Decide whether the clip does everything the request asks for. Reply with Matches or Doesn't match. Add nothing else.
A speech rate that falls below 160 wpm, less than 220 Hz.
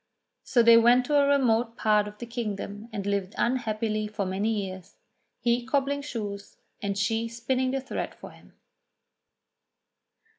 Doesn't match